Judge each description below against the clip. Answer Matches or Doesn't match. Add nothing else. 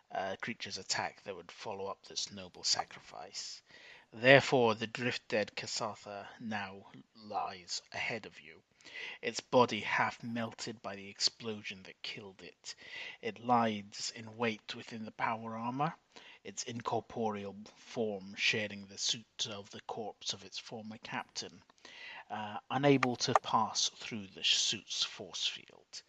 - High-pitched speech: Doesn't match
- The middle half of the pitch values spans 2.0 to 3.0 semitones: Doesn't match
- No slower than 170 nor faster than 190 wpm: Doesn't match